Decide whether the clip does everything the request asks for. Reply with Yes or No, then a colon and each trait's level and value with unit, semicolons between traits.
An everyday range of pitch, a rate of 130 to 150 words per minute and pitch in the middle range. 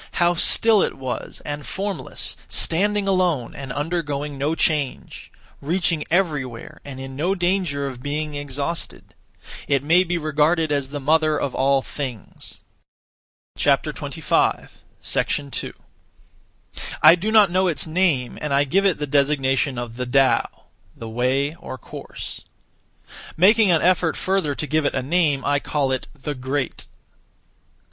Yes: average, 4.2 semitones; average, 140 wpm; medium, 150 Hz